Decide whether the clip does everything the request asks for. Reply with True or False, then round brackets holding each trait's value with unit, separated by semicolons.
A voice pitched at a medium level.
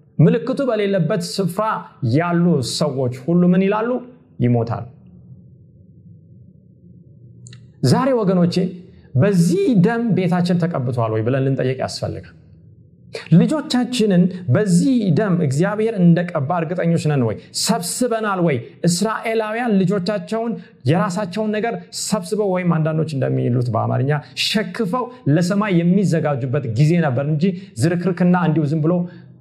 True (175 Hz)